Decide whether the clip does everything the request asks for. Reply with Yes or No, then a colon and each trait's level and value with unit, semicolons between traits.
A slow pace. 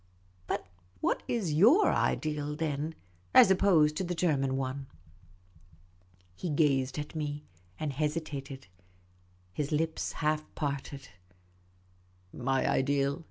Yes: slow, 115 wpm